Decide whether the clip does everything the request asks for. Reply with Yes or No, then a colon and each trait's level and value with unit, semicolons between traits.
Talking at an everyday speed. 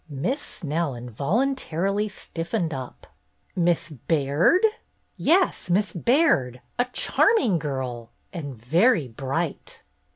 No: slow, 100 wpm